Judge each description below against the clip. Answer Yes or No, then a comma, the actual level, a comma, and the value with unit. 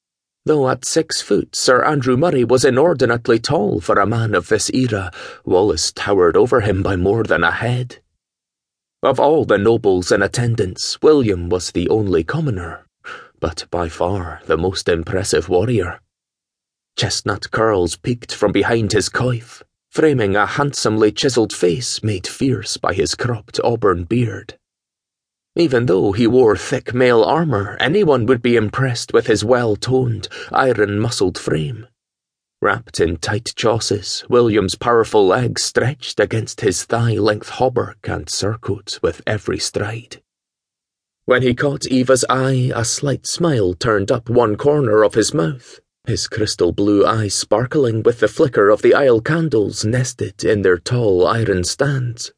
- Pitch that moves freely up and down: No, average, 3.8 semitones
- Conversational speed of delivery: Yes, average, 145 wpm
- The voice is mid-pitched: No, low, 120 Hz